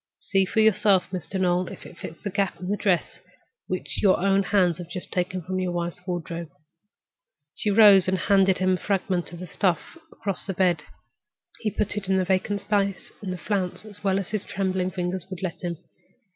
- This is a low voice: No, medium, 185 Hz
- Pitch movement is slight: Yes, narrow, 1.8 semitones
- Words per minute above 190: Yes, average, 200 wpm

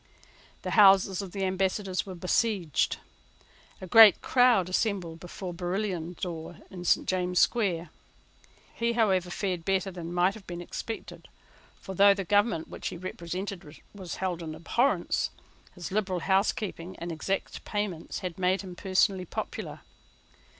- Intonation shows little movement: Yes, narrow, 2.3 semitones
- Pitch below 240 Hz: Yes, medium, 185 Hz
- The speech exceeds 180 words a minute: No, average, 145 wpm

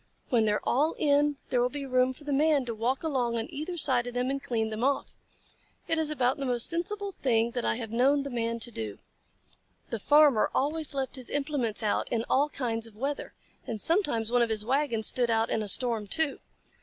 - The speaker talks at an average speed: No, fast, 225 wpm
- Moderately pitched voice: No, very high, 255 Hz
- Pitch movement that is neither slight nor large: Yes, average, 4.0 semitones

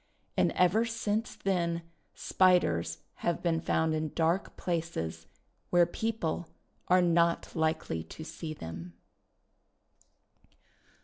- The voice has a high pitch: No, medium, 170 Hz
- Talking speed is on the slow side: Yes, slow, 105 wpm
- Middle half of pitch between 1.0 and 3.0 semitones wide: Yes, narrow, 2.4 semitones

